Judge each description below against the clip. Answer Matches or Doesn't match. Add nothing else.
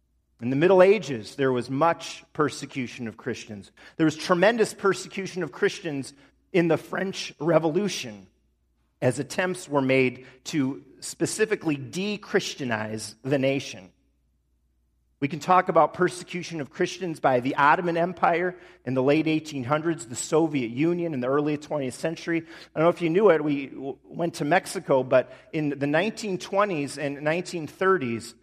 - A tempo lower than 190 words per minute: Matches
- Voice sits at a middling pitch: Matches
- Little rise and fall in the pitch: Doesn't match